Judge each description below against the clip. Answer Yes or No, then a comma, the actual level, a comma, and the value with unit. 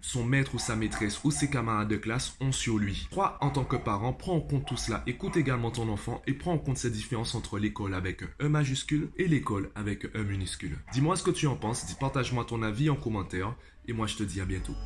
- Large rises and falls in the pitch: No, average, 4.6 semitones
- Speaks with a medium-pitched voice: No, low, 120 Hz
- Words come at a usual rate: No, fast, 250 wpm